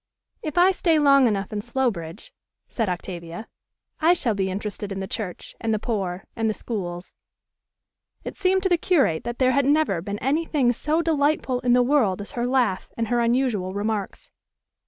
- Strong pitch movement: Yes, wide, 6.0 semitones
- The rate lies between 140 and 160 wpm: No, average, 185 wpm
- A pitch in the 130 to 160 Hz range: No, high, 235 Hz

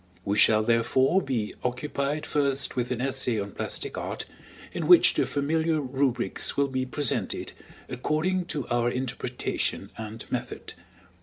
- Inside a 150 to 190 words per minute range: No, average, 140 wpm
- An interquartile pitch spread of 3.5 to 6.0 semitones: No, average, 3.1 semitones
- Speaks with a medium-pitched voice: No, low, 130 Hz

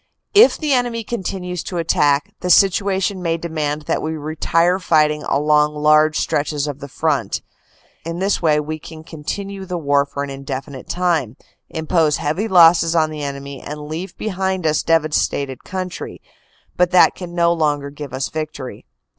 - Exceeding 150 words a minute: Yes, average, 165 wpm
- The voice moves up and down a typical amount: Yes, average, 3.4 semitones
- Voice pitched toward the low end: No, medium, 155 Hz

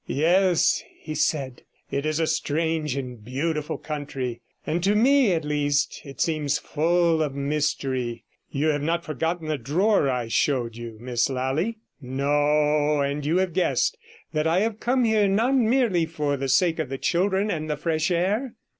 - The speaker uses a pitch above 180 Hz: No, medium, 155 Hz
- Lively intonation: No, average, 4.1 semitones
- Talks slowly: No, average, 165 wpm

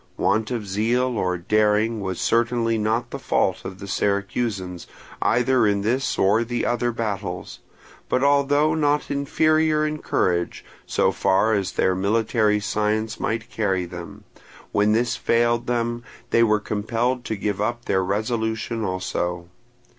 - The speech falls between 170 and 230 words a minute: No, average, 145 wpm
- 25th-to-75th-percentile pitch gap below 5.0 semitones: Yes, average, 3.1 semitones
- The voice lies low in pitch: Yes, low, 110 Hz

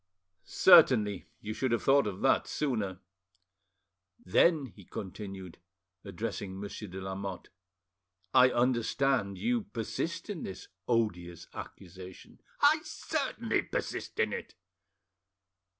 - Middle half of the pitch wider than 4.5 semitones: Yes, wide, 5.4 semitones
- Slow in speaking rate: Yes, slow, 105 wpm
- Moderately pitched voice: No, low, 105 Hz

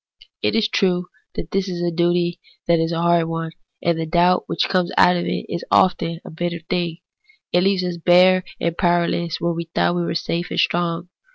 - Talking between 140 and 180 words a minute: No, fast, 205 wpm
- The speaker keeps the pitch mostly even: Yes, narrow, 1.0 semitones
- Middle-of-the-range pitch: Yes, medium, 175 Hz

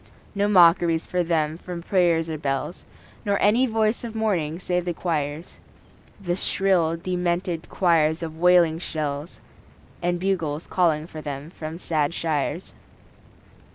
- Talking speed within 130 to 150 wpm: Yes, slow, 135 wpm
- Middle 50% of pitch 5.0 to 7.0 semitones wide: No, narrow, 2.5 semitones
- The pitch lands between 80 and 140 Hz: No, medium, 170 Hz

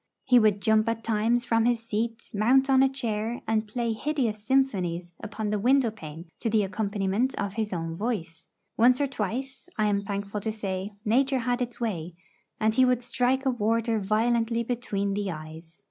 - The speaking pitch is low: No, high, 220 Hz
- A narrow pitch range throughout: No, average, 3.2 semitones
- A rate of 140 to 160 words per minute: No, average, 185 wpm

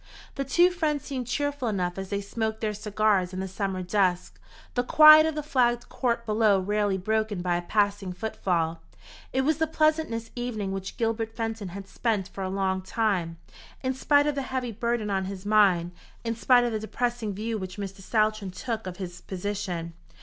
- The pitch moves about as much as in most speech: Yes, average, 4.1 semitones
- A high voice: Yes, high, 215 Hz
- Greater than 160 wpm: Yes, average, 190 wpm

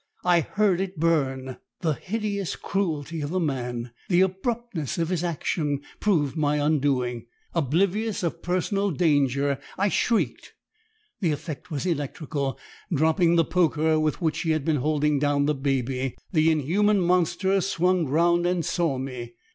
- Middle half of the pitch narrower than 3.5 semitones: No, average, 4.1 semitones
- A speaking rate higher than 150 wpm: No, average, 145 wpm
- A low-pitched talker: No, medium, 160 Hz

